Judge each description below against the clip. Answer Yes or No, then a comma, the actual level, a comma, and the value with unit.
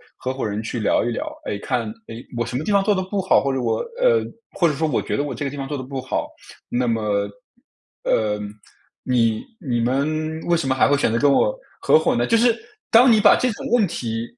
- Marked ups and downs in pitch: Yes, wide, 6.6 semitones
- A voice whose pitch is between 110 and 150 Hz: Yes, low, 135 Hz